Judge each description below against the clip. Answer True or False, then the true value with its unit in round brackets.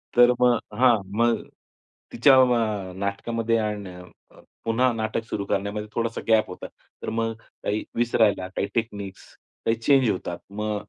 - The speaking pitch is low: True (110 Hz)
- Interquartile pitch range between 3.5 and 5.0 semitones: False (2.4 semitones)